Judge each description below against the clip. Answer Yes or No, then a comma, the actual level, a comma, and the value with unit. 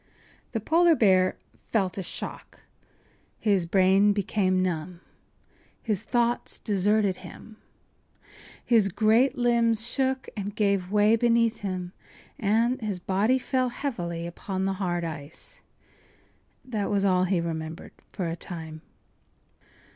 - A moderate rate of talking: No, slow, 125 wpm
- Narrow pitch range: No, average, 3.8 semitones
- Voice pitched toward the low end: No, high, 200 Hz